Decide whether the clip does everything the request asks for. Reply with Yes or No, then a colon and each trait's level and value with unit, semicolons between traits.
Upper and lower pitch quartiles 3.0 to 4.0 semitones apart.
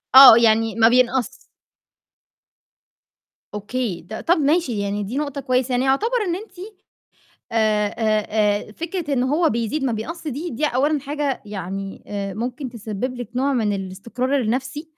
No: average, 4.8 semitones